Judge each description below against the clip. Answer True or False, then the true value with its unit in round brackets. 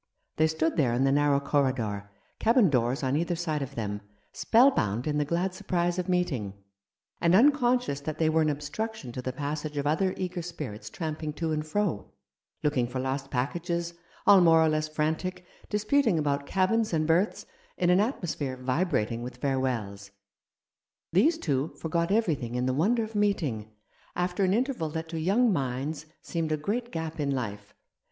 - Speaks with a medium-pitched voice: True (155 Hz)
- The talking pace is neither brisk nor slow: True (175 wpm)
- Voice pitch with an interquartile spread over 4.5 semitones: True (5.3 semitones)